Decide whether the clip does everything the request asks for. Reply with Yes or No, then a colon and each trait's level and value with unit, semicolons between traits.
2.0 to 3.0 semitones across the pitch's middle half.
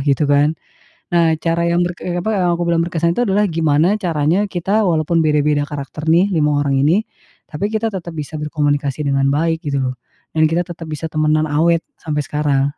Yes: average, 2.7 semitones